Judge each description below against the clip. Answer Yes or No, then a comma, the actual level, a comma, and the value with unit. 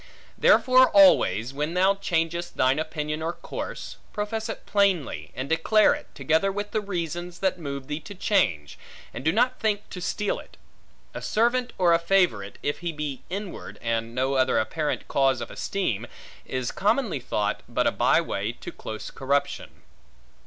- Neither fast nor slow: Yes, average, 165 wpm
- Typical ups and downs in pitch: No, wide, 6.7 semitones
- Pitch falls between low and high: Yes, medium, 165 Hz